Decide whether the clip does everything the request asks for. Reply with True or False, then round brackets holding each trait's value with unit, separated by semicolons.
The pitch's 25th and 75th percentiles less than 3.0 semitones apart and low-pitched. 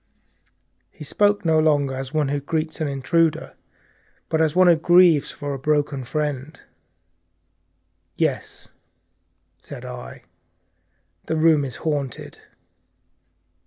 False (2.6 semitones; 150 Hz)